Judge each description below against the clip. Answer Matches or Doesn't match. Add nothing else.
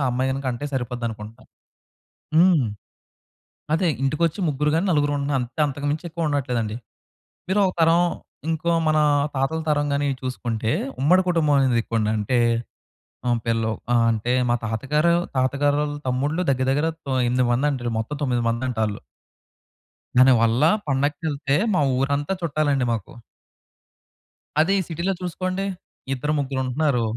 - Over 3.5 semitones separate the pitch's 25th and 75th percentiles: Matches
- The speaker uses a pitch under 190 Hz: Matches